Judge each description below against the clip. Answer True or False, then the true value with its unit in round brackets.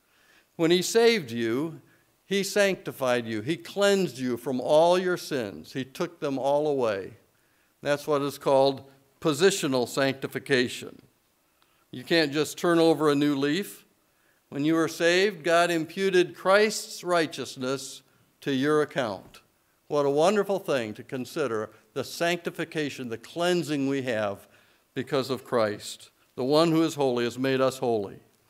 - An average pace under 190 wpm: True (145 wpm)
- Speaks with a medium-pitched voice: True (150 Hz)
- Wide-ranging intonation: False (4.4 semitones)